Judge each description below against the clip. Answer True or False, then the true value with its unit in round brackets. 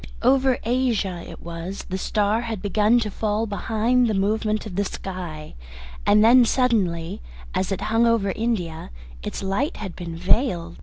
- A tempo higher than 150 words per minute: True (160 wpm)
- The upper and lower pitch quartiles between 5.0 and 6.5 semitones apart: False (3.8 semitones)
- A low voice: False (210 Hz)